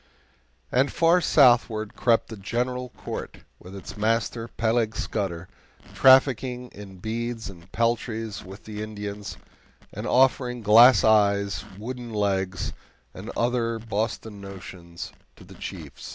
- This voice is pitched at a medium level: No, low, 110 Hz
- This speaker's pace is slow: Yes, slow, 125 wpm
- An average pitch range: Yes, average, 3.2 semitones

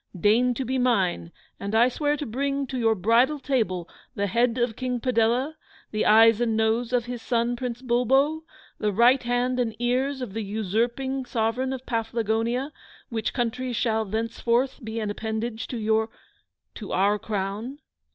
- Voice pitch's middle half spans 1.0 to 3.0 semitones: Yes, narrow, 2.4 semitones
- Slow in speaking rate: No, average, 165 wpm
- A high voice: Yes, high, 235 Hz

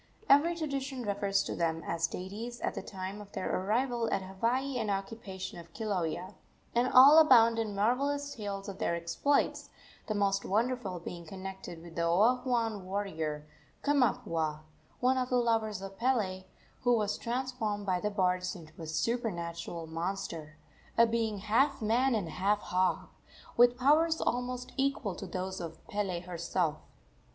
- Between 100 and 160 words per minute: Yes, average, 155 wpm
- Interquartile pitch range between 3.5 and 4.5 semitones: No, average, 5.0 semitones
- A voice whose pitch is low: No, high, 205 Hz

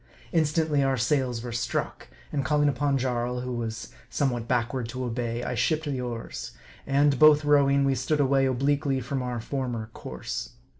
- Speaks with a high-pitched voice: No, low, 130 Hz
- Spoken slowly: No, average, 165 wpm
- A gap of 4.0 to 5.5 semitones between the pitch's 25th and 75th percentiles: No, average, 2.8 semitones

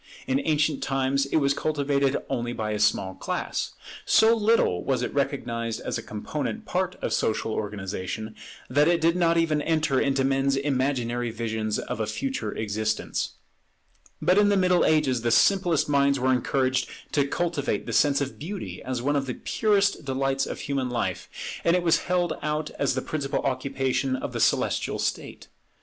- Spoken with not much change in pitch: No, average, 4.2 semitones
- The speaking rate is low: No, average, 175 wpm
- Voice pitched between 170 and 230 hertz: No, medium, 140 Hz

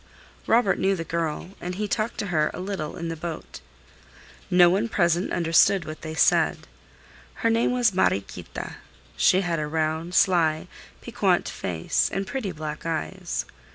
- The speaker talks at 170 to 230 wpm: No, average, 155 wpm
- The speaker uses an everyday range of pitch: Yes, average, 3.6 semitones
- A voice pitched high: No, medium, 170 Hz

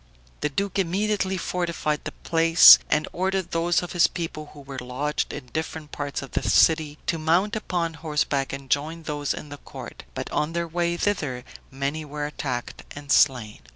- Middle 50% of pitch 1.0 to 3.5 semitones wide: Yes, average, 3.0 semitones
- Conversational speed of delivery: Yes, average, 180 wpm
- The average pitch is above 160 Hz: No, medium, 155 Hz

